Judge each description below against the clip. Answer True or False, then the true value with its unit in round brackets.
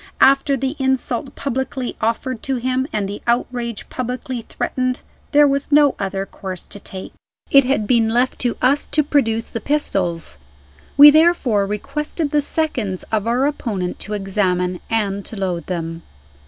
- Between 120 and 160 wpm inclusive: True (155 wpm)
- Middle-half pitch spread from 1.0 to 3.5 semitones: False (5.5 semitones)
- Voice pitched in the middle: False (240 Hz)